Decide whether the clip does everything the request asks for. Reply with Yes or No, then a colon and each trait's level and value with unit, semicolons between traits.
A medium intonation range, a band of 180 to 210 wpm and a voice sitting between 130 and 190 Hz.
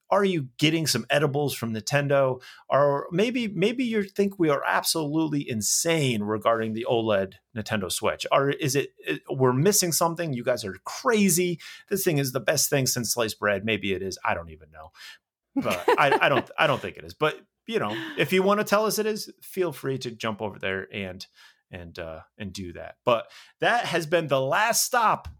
No: wide, 8.7 semitones; fast, 205 wpm; medium, 140 Hz